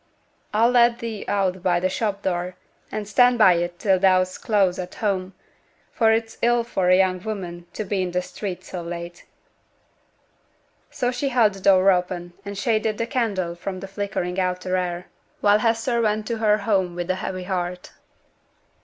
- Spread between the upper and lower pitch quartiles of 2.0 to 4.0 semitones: Yes, average, 3.2 semitones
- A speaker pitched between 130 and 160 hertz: No, high, 195 Hz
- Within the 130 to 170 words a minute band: No, average, 180 wpm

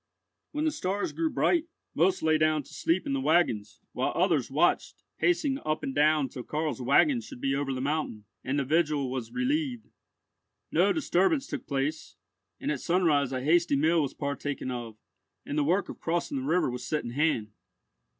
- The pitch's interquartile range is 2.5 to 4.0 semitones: No, average, 4.4 semitones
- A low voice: No, medium, 150 Hz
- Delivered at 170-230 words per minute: Yes, average, 190 wpm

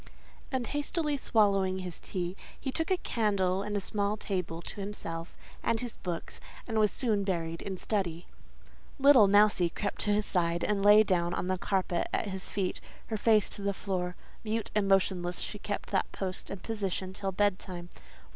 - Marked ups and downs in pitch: No, narrow, 2.6 semitones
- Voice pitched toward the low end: No, high, 195 Hz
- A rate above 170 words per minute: Yes, average, 185 wpm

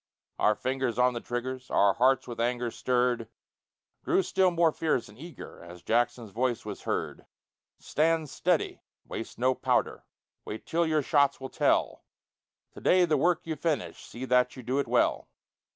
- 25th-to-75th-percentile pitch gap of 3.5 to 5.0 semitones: Yes, average, 4.3 semitones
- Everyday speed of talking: Yes, average, 170 wpm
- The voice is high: No, low, 130 Hz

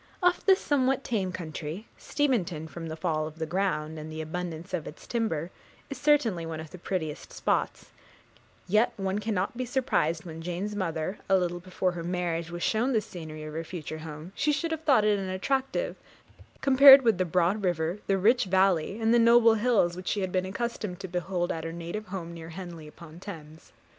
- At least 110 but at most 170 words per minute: No, average, 200 wpm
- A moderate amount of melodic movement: Yes, average, 5.0 semitones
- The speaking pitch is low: No, medium, 185 Hz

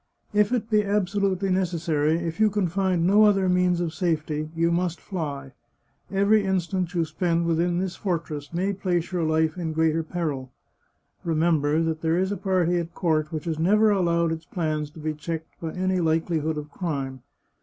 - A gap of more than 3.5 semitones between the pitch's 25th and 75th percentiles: No, average, 2.9 semitones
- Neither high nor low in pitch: Yes, medium, 170 Hz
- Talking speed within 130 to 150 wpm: No, average, 180 wpm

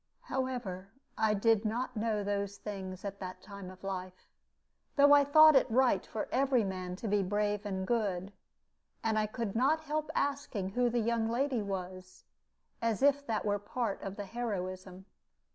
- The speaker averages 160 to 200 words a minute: Yes, average, 170 wpm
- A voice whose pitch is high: Yes, high, 210 Hz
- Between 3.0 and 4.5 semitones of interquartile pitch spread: Yes, average, 4.1 semitones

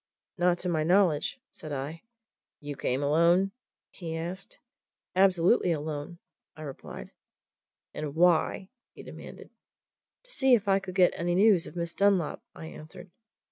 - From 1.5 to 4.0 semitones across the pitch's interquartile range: Yes, average, 3.4 semitones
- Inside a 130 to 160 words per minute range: Yes, average, 140 wpm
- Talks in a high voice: No, medium, 175 Hz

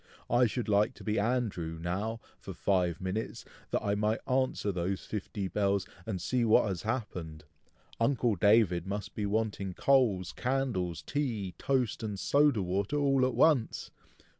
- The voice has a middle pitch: No, low, 105 Hz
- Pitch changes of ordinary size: Yes, average, 4.6 semitones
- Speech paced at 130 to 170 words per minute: Yes, average, 155 wpm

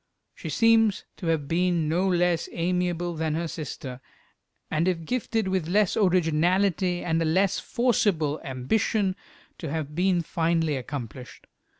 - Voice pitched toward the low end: No, medium, 170 Hz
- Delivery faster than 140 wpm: No, slow, 135 wpm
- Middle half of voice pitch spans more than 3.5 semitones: No, average, 3.1 semitones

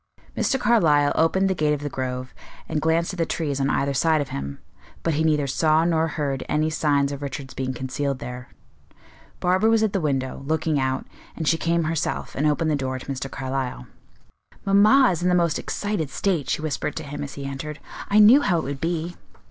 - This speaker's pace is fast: Yes, fast, 210 wpm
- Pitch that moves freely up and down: No, average, 3.6 semitones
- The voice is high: No, medium, 150 Hz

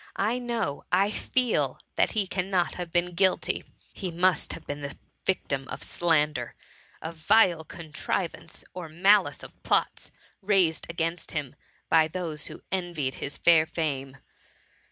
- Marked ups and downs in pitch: No, average, 3.3 semitones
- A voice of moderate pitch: Yes, medium, 170 Hz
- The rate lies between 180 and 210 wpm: No, average, 140 wpm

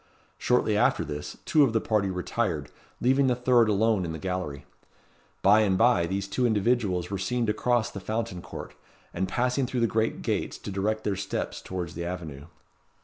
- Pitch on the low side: Yes, low, 105 Hz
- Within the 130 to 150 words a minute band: No, average, 190 wpm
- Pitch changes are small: No, average, 4.4 semitones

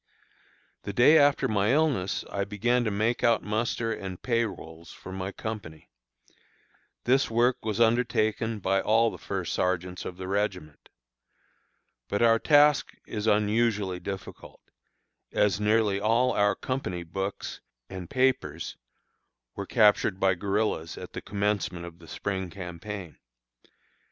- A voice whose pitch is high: No, low, 105 Hz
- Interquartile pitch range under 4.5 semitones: Yes, average, 3.6 semitones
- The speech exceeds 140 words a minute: No, slow, 135 wpm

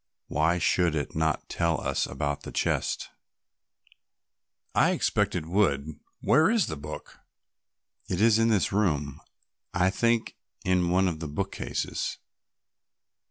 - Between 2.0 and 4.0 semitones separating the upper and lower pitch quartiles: No, average, 4.6 semitones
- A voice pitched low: Yes, very low, 90 Hz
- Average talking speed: No, slow, 130 wpm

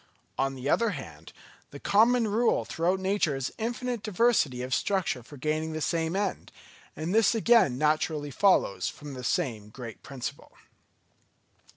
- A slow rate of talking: No, average, 150 wpm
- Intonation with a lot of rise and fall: Yes, wide, 7.4 semitones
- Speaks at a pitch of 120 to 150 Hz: No, medium, 160 Hz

